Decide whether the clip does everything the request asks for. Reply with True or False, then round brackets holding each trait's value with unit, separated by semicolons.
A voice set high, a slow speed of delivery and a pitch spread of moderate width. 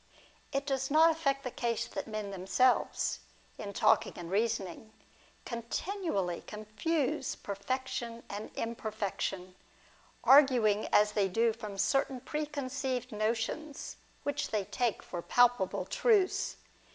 True (235 Hz; 115 wpm; 4.6 semitones)